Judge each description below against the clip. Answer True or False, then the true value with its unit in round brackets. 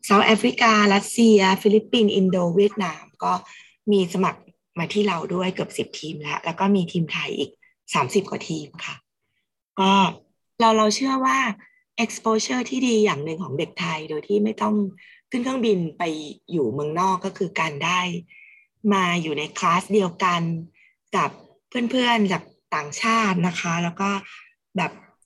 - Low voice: False (195 Hz)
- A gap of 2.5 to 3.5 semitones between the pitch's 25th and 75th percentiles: False (4.1 semitones)